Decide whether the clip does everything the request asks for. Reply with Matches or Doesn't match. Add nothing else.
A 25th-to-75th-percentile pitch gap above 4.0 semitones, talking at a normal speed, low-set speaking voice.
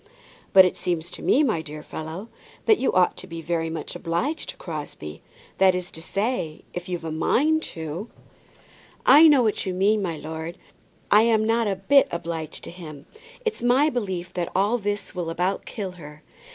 Doesn't match